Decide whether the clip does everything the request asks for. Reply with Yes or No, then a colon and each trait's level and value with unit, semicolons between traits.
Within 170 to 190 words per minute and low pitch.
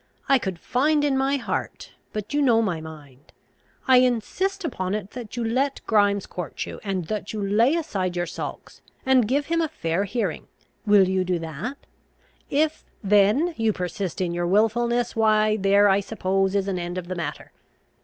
No: average, 185 wpm; high, 210 Hz